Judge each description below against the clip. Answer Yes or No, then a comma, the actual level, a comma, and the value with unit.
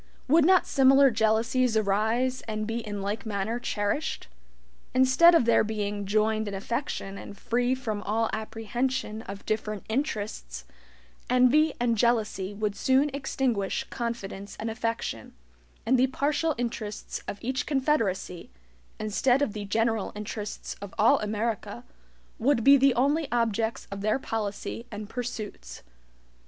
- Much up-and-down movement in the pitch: No, average, 3.6 semitones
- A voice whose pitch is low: No, high, 225 Hz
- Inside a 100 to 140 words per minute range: Yes, slow, 135 wpm